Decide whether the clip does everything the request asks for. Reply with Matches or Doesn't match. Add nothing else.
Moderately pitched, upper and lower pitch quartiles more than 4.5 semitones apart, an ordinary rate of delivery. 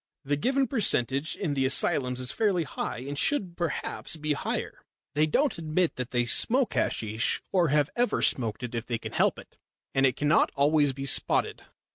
Matches